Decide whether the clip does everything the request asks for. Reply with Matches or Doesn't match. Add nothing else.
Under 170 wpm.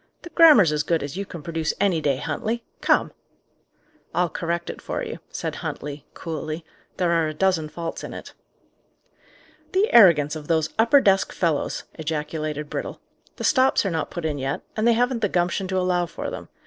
Doesn't match